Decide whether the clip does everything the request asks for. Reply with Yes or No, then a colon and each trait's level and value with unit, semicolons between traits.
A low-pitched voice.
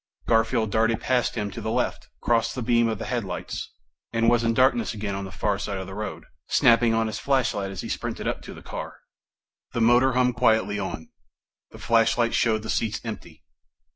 Yes: low, 115 Hz